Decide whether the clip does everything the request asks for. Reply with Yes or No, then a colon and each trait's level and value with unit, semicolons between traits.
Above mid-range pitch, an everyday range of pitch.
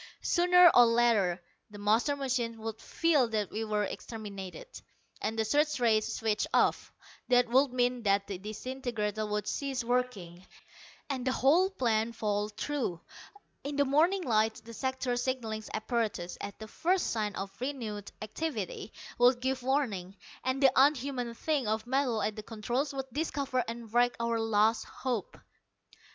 Yes: high, 235 Hz; average, 3.6 semitones